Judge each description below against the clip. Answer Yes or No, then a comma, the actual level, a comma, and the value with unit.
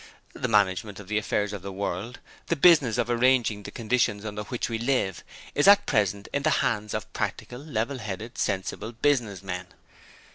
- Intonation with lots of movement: No, average, 3.8 semitones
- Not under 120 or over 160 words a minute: No, average, 180 wpm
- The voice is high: No, low, 110 Hz